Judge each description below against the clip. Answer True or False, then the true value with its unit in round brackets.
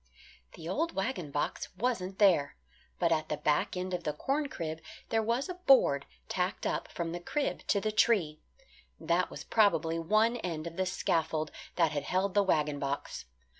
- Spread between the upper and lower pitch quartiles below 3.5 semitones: False (5.1 semitones)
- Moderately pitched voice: True (180 Hz)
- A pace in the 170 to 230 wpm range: True (180 wpm)